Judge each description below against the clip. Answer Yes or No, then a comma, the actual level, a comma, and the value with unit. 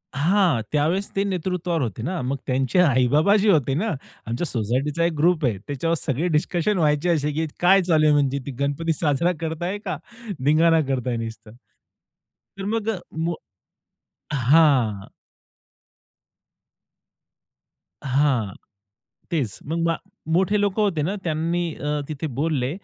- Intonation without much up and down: No, average, 4.2 semitones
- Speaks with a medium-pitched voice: Yes, medium, 155 Hz